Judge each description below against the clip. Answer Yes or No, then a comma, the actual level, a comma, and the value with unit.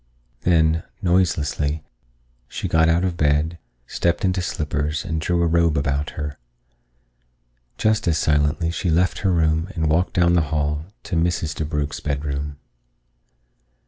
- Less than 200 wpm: Yes, average, 140 wpm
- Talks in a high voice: No, very low, 80 Hz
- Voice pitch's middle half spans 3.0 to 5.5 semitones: No, narrow, 2.5 semitones